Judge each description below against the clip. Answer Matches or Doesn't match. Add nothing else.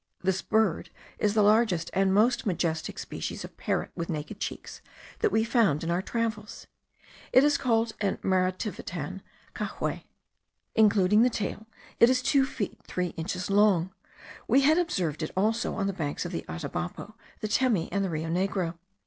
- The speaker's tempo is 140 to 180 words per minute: Matches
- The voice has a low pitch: Doesn't match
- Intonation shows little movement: Doesn't match